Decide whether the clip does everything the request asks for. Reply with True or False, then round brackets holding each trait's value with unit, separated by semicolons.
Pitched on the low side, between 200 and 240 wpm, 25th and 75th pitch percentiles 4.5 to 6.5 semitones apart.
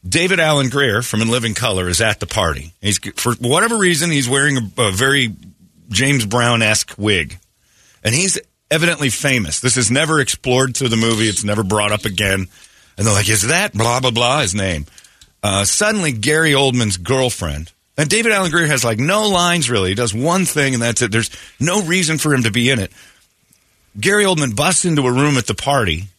True (120 Hz; 205 wpm; 5.6 semitones)